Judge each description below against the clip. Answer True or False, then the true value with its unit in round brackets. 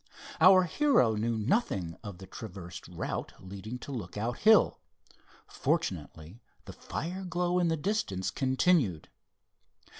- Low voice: True (120 Hz)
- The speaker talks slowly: True (120 wpm)